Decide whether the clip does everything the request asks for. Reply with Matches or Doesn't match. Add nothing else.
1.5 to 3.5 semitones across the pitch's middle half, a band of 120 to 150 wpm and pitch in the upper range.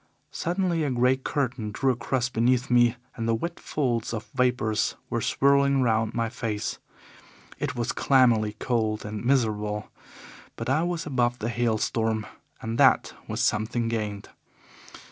Doesn't match